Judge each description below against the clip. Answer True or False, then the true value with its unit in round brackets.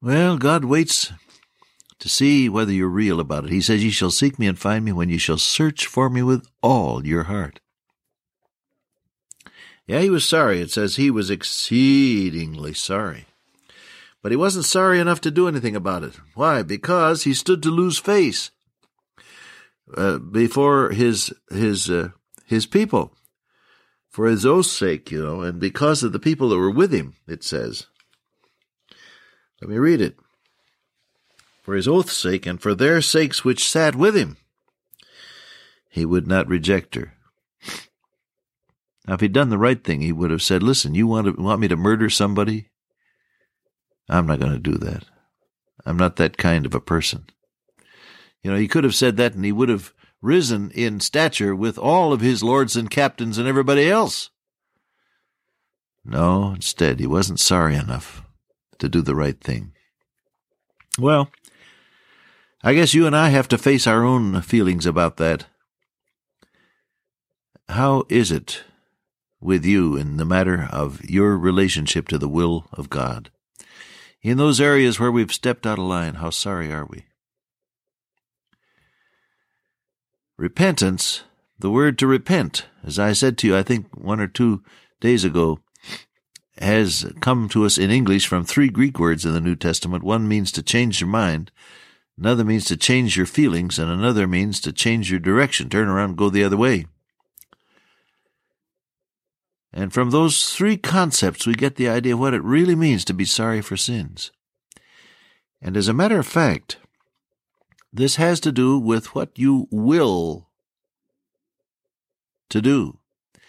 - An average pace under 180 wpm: True (160 wpm)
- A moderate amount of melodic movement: False (6.8 semitones)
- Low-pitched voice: True (110 Hz)